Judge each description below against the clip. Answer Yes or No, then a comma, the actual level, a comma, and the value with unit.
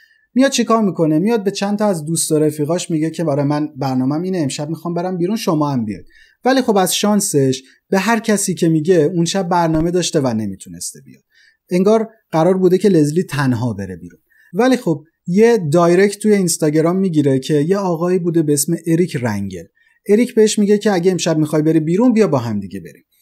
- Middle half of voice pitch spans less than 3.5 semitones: No, average, 5.2 semitones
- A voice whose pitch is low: No, medium, 170 Hz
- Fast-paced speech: Yes, fast, 200 wpm